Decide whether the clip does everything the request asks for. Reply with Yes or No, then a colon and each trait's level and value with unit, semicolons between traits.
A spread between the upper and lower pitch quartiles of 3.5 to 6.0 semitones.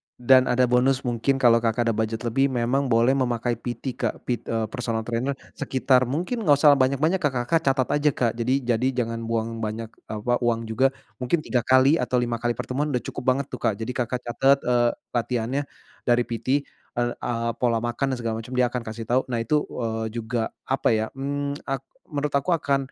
No: average, 2.7 semitones